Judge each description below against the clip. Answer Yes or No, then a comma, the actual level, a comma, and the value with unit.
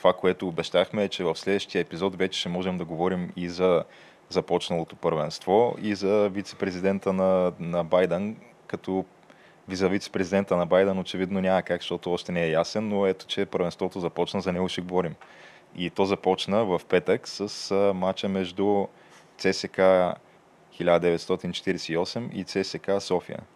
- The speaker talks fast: No, average, 150 wpm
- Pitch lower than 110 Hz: Yes, very low, 95 Hz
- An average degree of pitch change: No, narrow, 1.6 semitones